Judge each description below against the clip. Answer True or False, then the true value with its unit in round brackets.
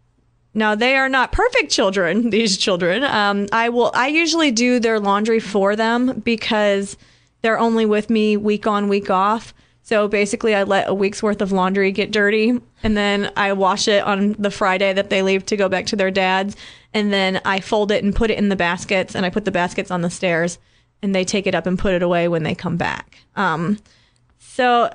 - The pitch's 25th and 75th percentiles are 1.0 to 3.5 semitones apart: True (2.7 semitones)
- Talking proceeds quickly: True (215 wpm)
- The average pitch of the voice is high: True (205 Hz)